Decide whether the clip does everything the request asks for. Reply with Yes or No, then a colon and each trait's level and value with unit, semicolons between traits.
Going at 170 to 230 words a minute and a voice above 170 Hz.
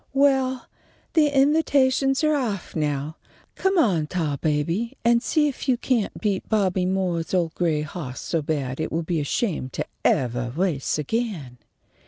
No: average, 150 wpm; medium, 185 Hz